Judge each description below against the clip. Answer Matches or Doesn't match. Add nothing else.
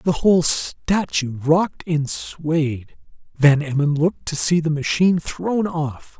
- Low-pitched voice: Doesn't match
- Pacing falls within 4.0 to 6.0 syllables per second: Doesn't match